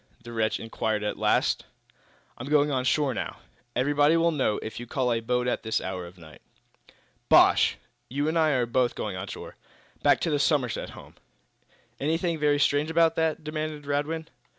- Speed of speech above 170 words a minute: Yes, average, 185 wpm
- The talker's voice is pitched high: No, medium, 140 Hz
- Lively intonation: No, average, 4.8 semitones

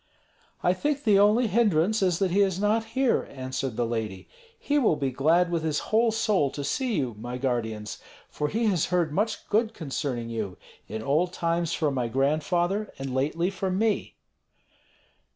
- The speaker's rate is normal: Yes, average, 175 wpm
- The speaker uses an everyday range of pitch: No, wide, 7.7 semitones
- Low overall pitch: No, medium, 170 Hz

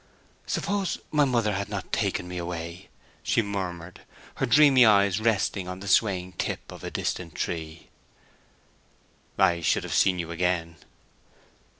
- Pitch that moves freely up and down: No, average, 3.7 semitones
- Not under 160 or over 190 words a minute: No, average, 140 wpm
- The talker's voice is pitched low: Yes, very low, 90 Hz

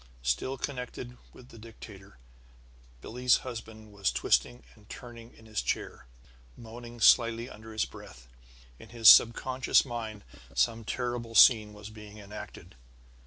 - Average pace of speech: No, slow, 130 wpm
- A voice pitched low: Yes, low, 115 Hz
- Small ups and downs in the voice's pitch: Yes, narrow, 2.2 semitones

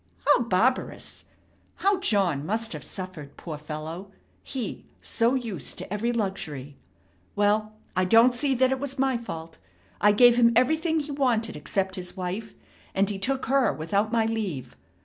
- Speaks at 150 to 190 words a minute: Yes, average, 160 wpm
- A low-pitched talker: No, high, 215 Hz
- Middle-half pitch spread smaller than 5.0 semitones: No, average, 5.3 semitones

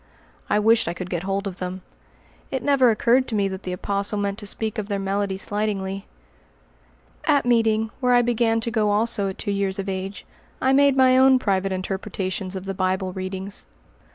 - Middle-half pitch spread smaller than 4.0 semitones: Yes, average, 3.2 semitones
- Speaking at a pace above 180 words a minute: Yes, average, 195 wpm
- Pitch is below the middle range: No, high, 200 Hz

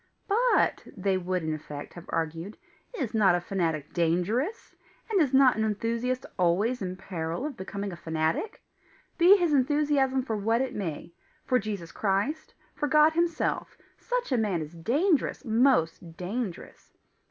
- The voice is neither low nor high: No, high, 215 Hz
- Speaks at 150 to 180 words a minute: Yes, average, 155 wpm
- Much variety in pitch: Yes, wide, 7.9 semitones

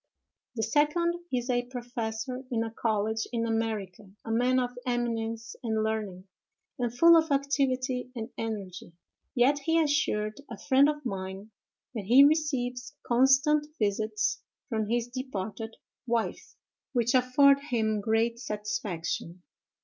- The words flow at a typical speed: No, slow, 125 wpm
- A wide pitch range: No, average, 3.2 semitones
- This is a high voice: Yes, high, 240 Hz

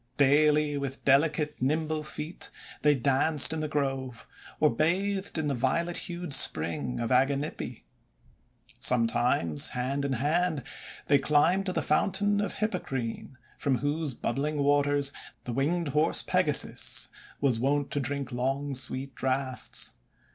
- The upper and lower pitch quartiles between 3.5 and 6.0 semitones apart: No, average, 2.8 semitones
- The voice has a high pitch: No, medium, 140 Hz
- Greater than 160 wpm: No, slow, 135 wpm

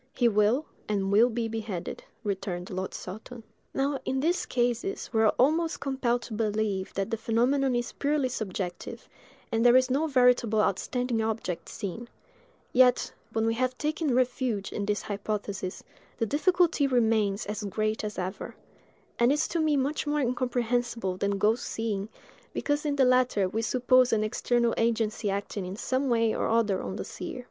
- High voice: Yes, high, 230 Hz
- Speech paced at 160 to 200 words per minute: Yes, average, 170 wpm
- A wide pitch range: No, average, 3.5 semitones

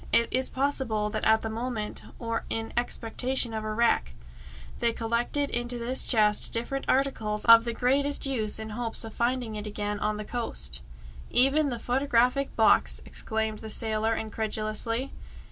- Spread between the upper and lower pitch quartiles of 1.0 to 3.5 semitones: Yes, narrow, 2.5 semitones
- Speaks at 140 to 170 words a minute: Yes, average, 160 wpm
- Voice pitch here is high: Yes, high, 230 Hz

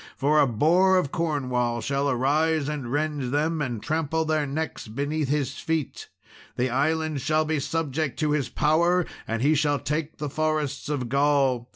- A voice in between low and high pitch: Yes, medium, 150 Hz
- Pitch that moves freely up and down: No, narrow, 2.6 semitones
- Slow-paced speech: No, average, 170 wpm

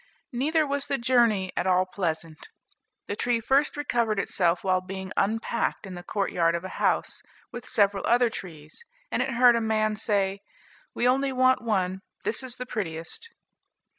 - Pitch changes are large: No, average, 4.9 semitones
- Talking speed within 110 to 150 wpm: No, average, 170 wpm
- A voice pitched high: Yes, high, 215 Hz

